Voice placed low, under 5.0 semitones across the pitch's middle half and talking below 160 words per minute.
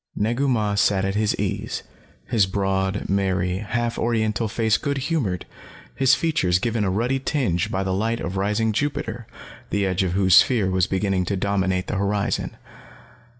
No: low, 100 Hz; average, 3.4 semitones; average, 165 wpm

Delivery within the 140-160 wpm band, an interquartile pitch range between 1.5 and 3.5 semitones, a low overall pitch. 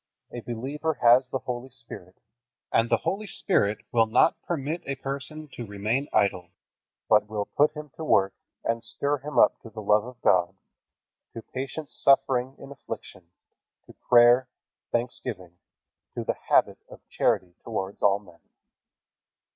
No: average, 150 wpm; average, 4.7 semitones; low, 120 Hz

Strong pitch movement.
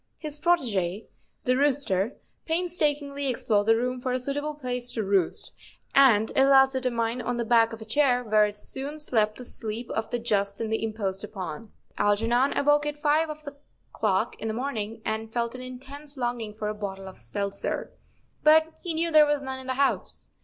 No: average, 4.6 semitones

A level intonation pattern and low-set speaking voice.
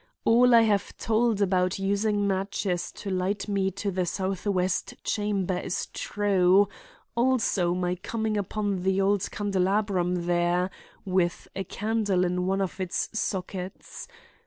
No: narrow, 2.2 semitones; high, 195 Hz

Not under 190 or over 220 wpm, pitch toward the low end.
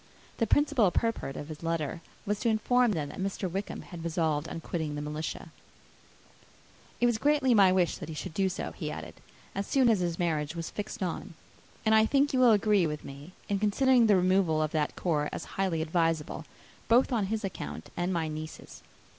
No: average, 200 wpm; medium, 185 Hz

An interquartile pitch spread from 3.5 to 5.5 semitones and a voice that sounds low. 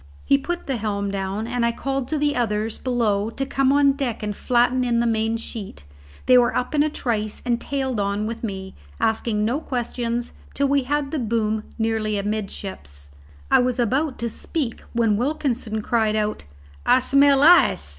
No: average, 4.0 semitones; high, 235 Hz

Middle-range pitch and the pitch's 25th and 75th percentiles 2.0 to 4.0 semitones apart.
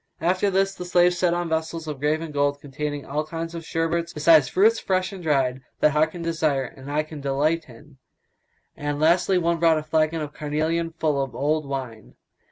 Yes: medium, 155 Hz; narrow, 2.6 semitones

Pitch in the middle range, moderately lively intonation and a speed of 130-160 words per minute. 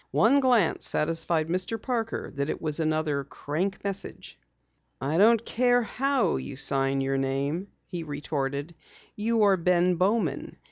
No: medium, 170 Hz; wide, 7.1 semitones; average, 140 wpm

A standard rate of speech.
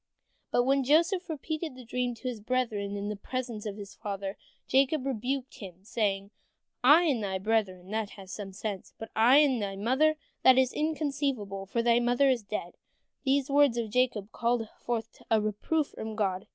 Yes: average, 185 wpm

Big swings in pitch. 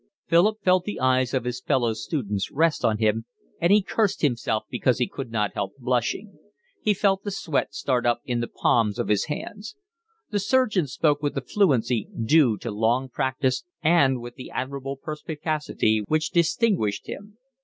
Yes: wide, 6.3 semitones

